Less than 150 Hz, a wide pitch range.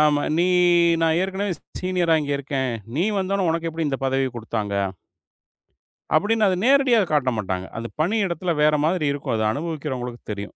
No: medium, 155 Hz; wide, 5.7 semitones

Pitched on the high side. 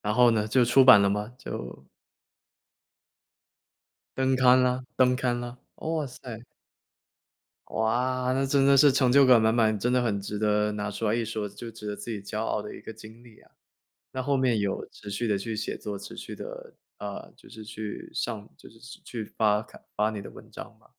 No: low, 115 Hz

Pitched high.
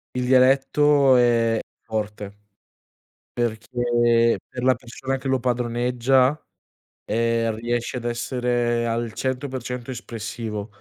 No: low, 120 Hz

